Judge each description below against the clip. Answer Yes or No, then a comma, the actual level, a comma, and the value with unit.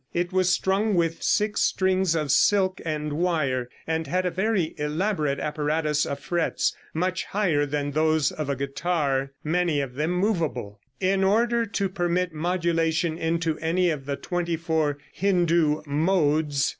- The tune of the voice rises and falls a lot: No, average, 3.6 semitones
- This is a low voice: No, medium, 165 Hz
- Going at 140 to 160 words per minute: Yes, average, 150 wpm